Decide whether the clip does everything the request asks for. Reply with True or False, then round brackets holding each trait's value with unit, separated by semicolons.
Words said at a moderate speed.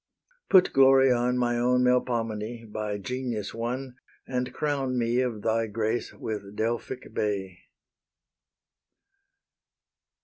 False (105 wpm)